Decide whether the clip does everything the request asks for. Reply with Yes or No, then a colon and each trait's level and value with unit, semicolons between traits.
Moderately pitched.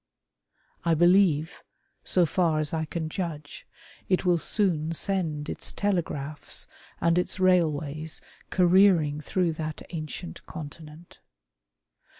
Yes: medium, 165 Hz